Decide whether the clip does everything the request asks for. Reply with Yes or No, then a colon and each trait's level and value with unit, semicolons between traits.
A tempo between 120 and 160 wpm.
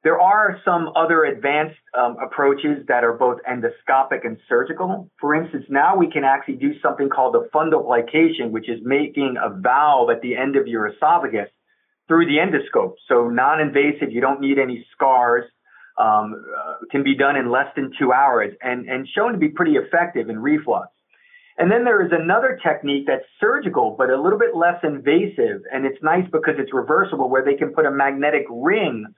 No: average, 190 wpm